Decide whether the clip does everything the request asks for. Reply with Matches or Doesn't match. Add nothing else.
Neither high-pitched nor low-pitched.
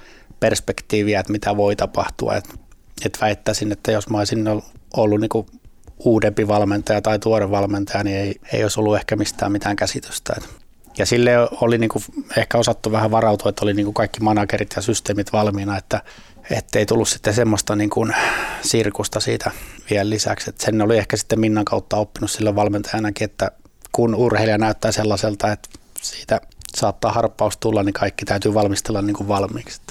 Doesn't match